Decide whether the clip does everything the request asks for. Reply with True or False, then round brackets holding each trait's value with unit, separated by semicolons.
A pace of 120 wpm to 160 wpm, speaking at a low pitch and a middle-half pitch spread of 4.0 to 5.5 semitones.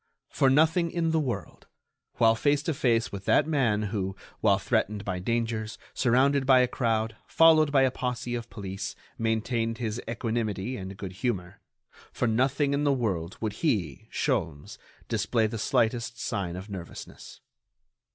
True (155 wpm; 115 Hz; 4.4 semitones)